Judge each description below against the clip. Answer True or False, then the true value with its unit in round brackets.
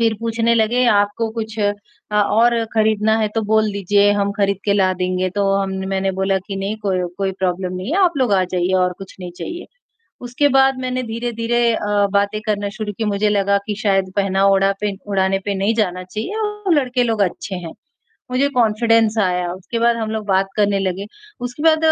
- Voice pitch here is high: True (205 Hz)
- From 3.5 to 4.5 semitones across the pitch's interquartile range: False (2.8 semitones)